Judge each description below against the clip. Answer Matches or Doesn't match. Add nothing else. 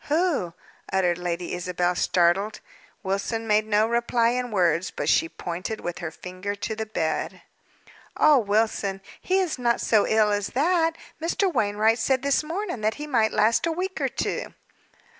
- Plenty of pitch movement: Matches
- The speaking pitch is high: Matches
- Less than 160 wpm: Doesn't match